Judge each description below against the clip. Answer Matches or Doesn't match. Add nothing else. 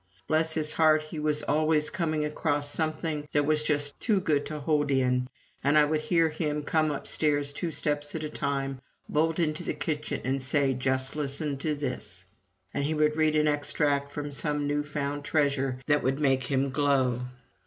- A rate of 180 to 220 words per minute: Matches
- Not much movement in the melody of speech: Matches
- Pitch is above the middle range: Doesn't match